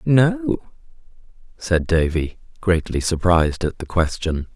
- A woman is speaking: No, male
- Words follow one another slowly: Yes, slow, 105 wpm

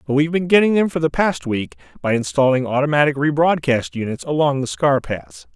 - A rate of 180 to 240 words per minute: Yes, fast, 205 wpm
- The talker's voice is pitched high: No, medium, 140 Hz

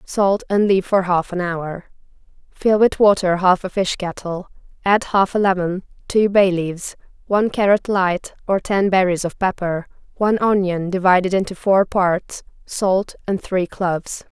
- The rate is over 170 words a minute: No, average, 165 wpm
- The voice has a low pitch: No, high, 190 Hz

